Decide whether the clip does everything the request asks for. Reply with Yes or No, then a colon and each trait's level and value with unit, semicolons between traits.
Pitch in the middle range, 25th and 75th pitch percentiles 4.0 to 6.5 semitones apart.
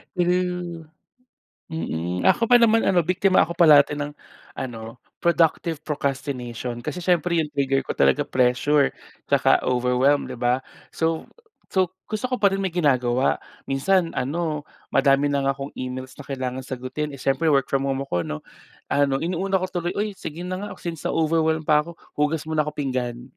Yes: medium, 150 Hz; average, 4.6 semitones